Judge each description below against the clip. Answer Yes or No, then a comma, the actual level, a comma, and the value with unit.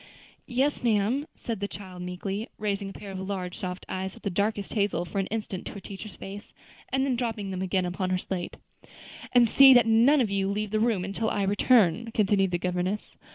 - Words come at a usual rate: No, fast, 210 wpm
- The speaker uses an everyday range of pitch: Yes, average, 3.0 semitones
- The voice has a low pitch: No, high, 200 Hz